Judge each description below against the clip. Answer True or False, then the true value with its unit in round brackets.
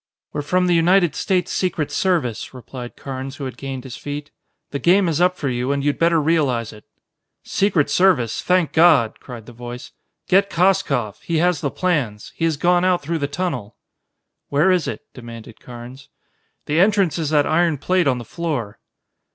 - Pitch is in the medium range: True (150 Hz)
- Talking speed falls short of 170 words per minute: False (185 wpm)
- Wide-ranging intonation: True (5.7 semitones)